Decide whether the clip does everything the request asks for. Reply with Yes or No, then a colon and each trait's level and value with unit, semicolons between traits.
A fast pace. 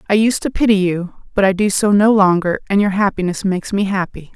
Yes: fast, 235 wpm